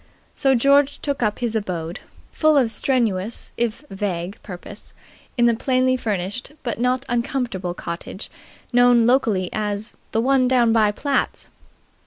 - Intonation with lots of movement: No, average, 3.8 semitones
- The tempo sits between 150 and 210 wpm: No, average, 140 wpm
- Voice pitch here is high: Yes, high, 235 Hz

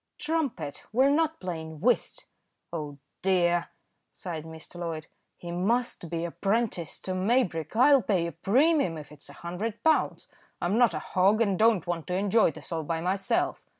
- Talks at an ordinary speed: Yes, average, 170 wpm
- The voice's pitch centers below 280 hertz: Yes, medium, 185 Hz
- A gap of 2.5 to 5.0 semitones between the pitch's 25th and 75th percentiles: No, wide, 5.6 semitones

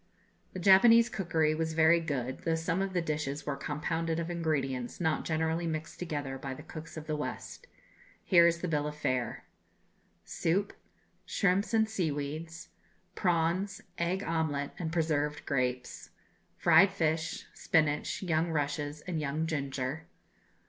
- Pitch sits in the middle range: Yes, medium, 160 Hz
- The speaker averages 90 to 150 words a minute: Yes, average, 140 wpm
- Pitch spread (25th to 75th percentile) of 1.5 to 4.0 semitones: Yes, narrow, 2.5 semitones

